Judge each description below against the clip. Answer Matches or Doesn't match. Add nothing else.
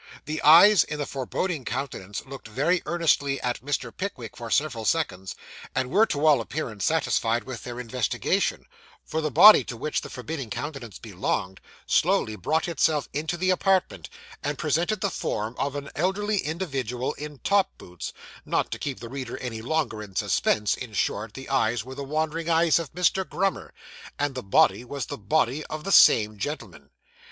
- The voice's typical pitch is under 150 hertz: Matches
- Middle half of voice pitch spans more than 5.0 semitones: Matches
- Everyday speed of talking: Matches